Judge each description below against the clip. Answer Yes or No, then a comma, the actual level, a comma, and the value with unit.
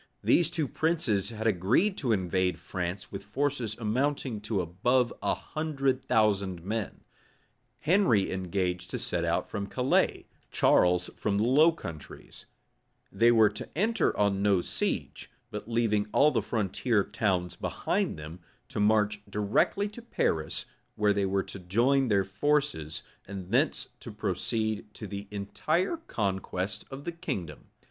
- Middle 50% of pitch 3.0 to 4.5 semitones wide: No, wide, 5.4 semitones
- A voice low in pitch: Yes, low, 105 Hz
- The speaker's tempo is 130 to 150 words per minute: Yes, average, 145 wpm